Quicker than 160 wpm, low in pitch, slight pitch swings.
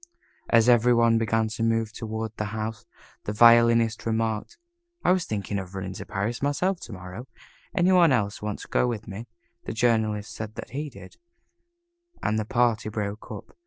Yes: average, 185 wpm; low, 110 Hz; narrow, 1.9 semitones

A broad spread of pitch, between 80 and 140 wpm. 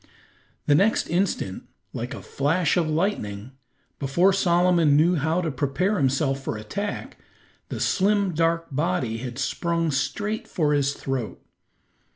No: average, 5.0 semitones; slow, 135 wpm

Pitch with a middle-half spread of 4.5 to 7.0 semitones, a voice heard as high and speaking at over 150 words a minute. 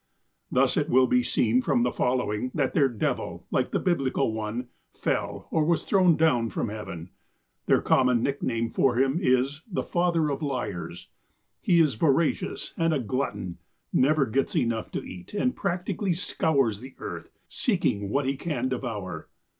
No: average, 5.2 semitones; low, 130 Hz; average, 160 wpm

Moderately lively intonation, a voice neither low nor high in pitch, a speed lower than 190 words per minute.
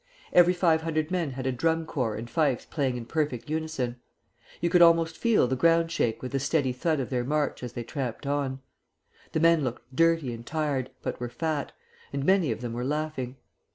No: average, 4.5 semitones; medium, 145 Hz; fast, 205 wpm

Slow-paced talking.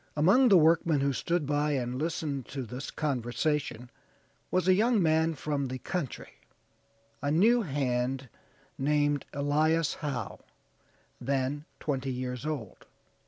Yes: slow, 125 wpm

